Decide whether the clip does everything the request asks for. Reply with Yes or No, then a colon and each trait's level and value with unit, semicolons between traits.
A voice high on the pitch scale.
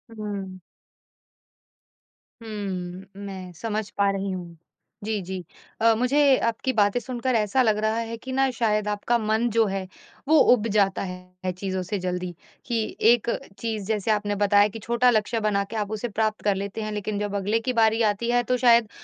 Yes: high, 210 Hz